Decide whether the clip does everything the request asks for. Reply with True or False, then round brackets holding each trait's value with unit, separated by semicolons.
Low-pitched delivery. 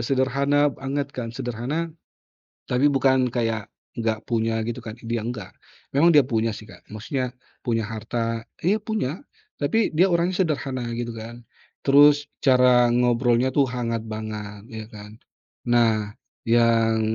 True (120 Hz)